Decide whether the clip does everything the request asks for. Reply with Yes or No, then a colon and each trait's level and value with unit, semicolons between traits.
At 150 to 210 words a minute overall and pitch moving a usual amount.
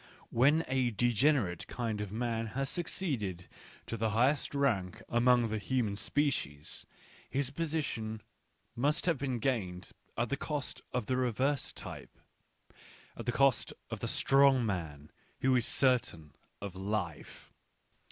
No: average, 140 wpm; average, 4.7 semitones